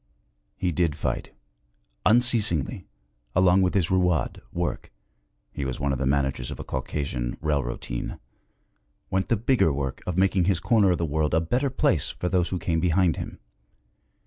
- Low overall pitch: Yes, very low, 85 Hz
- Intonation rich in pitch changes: No, average, 4.7 semitones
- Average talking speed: Yes, average, 165 wpm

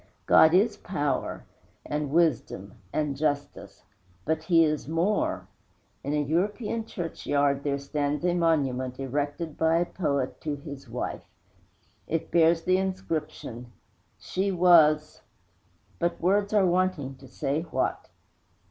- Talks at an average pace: No, slow, 125 wpm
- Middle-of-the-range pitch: Yes, medium, 155 Hz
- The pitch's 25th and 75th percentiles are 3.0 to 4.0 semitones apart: Yes, average, 3.7 semitones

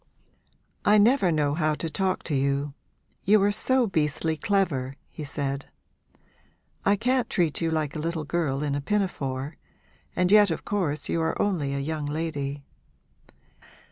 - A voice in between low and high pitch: Yes, medium, 160 Hz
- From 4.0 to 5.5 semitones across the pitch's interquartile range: Yes, average, 5.1 semitones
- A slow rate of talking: No, average, 155 wpm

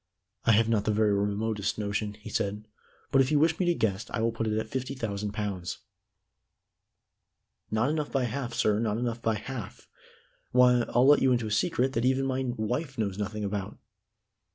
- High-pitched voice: No, low, 110 Hz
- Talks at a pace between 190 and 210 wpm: Yes, average, 195 wpm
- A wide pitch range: No, average, 3.6 semitones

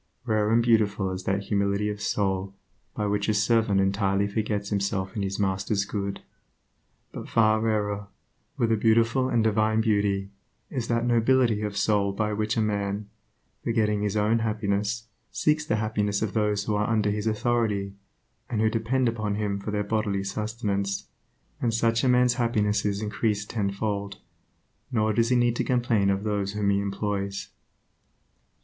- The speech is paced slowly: No, average, 165 wpm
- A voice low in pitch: Yes, low, 105 Hz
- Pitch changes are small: Yes, narrow, 2.0 semitones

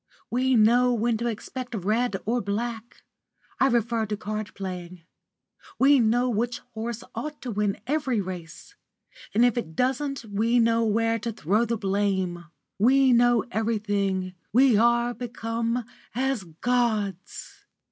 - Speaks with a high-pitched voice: Yes, high, 230 Hz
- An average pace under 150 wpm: Yes, slow, 135 wpm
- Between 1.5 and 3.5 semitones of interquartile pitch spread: Yes, average, 2.9 semitones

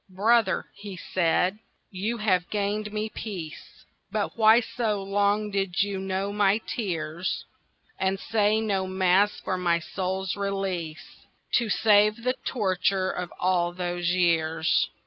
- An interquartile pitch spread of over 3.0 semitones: No, narrow, 2.6 semitones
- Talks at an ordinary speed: No, slow, 130 wpm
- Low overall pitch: No, high, 195 Hz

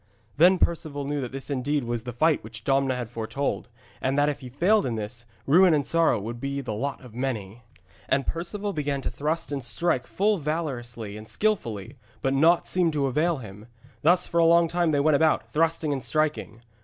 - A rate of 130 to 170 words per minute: No, fast, 205 wpm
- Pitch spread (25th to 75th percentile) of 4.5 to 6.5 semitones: Yes, average, 5.2 semitones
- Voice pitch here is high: No, medium, 140 Hz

